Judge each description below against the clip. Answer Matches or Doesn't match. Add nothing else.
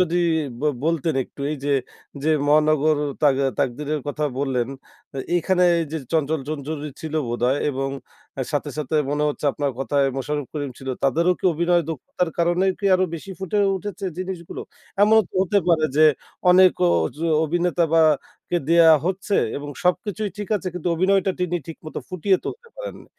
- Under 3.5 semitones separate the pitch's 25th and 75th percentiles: Doesn't match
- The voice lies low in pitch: Doesn't match